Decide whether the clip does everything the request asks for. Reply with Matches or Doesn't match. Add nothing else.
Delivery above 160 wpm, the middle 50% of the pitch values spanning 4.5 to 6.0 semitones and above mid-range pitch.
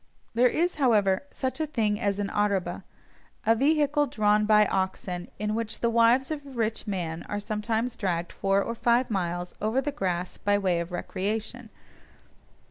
Doesn't match